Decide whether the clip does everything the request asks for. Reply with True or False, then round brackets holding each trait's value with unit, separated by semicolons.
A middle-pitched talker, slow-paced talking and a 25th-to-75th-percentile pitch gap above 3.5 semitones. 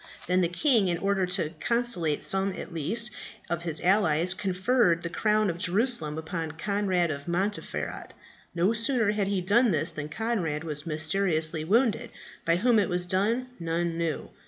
False (180 Hz; 165 wpm; 4.3 semitones)